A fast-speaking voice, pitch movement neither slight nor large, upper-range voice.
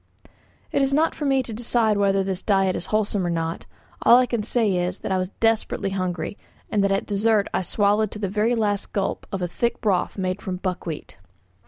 Yes: fast, 215 wpm; average, 3.1 semitones; high, 200 Hz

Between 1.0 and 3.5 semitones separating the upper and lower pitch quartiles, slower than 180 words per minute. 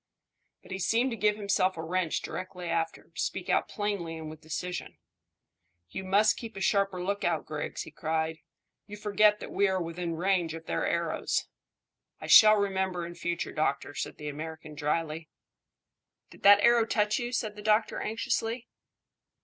No: average, 4.3 semitones; average, 170 wpm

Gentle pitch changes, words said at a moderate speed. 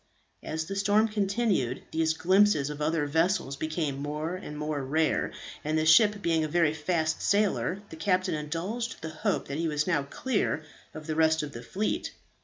No: average, 4.2 semitones; average, 185 wpm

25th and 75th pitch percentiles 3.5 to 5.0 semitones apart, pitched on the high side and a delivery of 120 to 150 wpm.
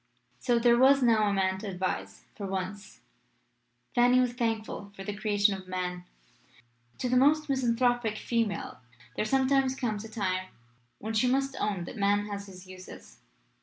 No: average, 4.2 semitones; high, 215 Hz; average, 165 wpm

